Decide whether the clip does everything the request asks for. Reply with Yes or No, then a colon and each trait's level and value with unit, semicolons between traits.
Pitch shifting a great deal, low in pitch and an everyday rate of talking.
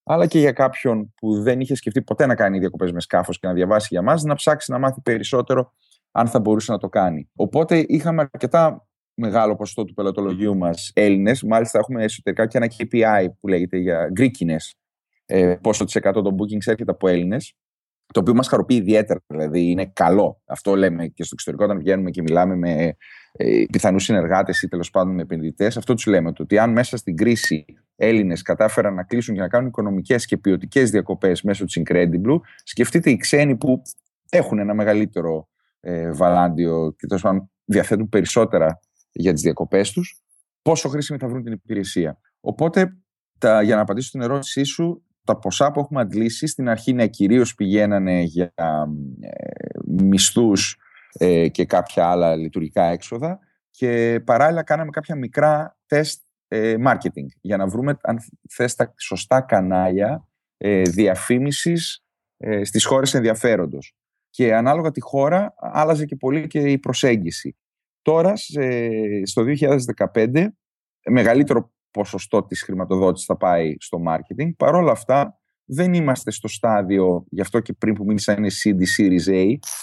Yes: wide, 6.0 semitones; low, 110 Hz; average, 160 wpm